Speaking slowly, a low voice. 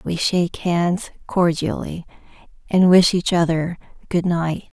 No: slow, 125 wpm; medium, 175 Hz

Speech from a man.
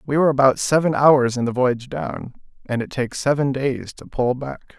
Yes: male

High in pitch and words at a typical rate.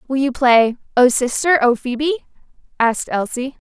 Yes: very high, 260 Hz; average, 145 wpm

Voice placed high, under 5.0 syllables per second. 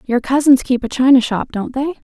No: very high, 260 Hz; 5.2 syllables/s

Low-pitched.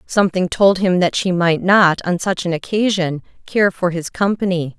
No: medium, 180 Hz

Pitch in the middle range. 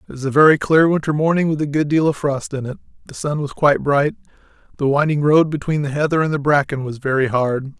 Yes: medium, 145 Hz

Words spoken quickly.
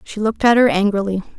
Yes: fast, 215 wpm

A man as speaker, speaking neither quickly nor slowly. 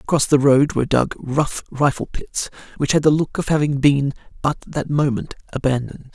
Yes: male; average, 185 wpm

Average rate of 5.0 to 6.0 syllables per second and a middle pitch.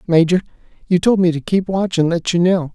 Yes: 5.6 syllables/s; medium, 175 Hz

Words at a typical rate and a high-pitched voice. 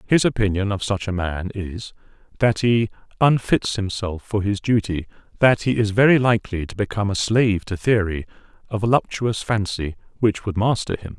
No: average, 165 wpm; low, 105 Hz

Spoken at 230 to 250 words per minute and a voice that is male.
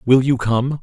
No: fast, 220 wpm; male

